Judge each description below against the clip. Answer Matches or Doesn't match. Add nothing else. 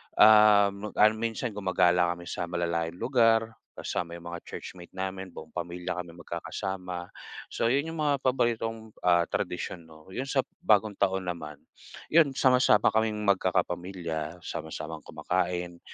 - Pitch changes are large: Doesn't match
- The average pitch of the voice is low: Matches